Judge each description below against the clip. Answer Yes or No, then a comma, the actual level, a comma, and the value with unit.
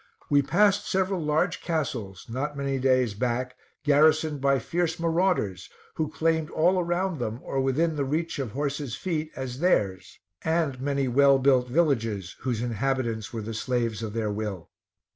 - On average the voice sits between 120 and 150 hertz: Yes, medium, 140 Hz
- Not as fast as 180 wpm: Yes, average, 160 wpm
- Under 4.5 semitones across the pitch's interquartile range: No, average, 5.1 semitones